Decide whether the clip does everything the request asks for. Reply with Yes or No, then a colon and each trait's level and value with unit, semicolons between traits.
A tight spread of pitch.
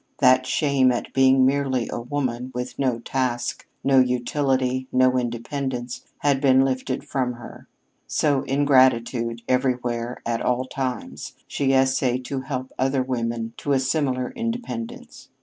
Yes: narrow, 1.5 semitones